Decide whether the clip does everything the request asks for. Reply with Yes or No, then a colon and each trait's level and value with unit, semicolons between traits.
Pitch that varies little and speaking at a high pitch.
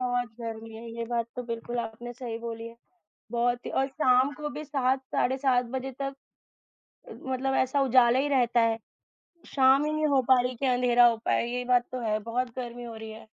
Yes: narrow, 2.1 semitones; high, 245 Hz